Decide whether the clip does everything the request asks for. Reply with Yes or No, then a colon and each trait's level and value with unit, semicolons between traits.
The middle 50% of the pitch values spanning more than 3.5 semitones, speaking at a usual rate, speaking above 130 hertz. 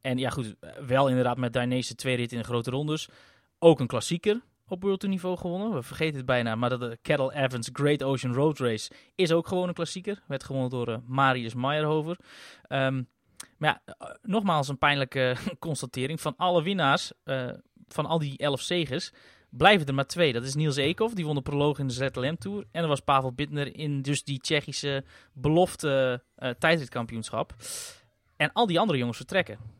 Yes: average, 4.3 semitones; average, 185 wpm; medium, 140 Hz